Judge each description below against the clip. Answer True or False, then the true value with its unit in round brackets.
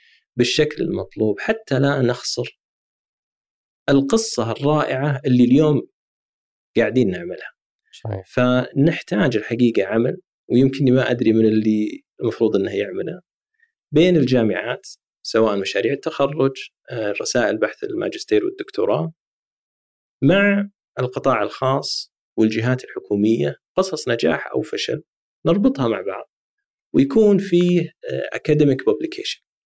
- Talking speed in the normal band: True (95 wpm)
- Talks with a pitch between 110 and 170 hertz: True (140 Hz)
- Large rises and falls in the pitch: True (8.7 semitones)